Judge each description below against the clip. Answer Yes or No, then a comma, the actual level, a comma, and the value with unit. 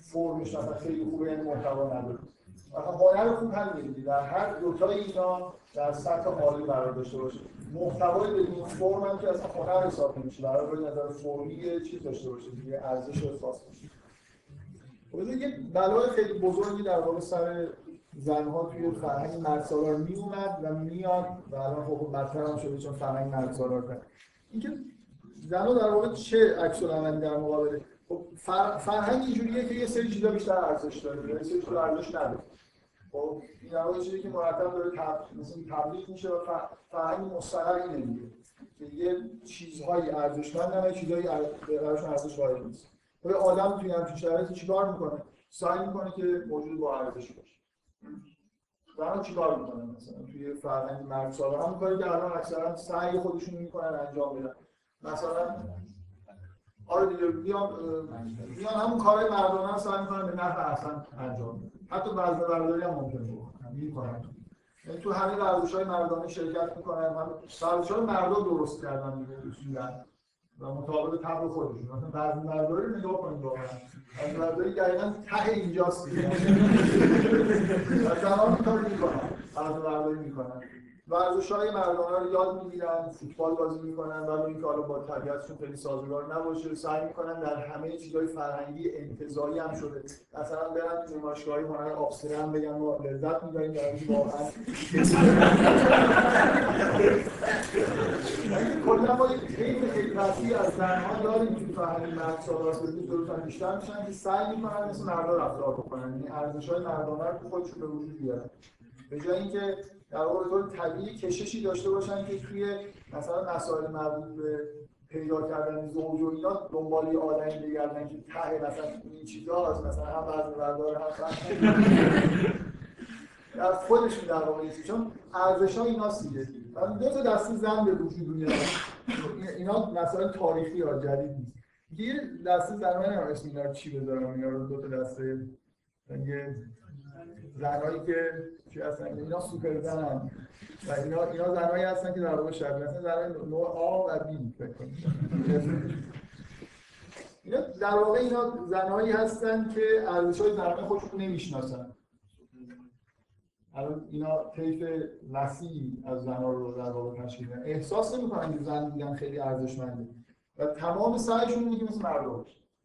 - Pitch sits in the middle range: Yes, medium, 160 Hz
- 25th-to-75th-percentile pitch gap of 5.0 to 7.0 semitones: No, average, 4.3 semitones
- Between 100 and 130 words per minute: No, average, 145 wpm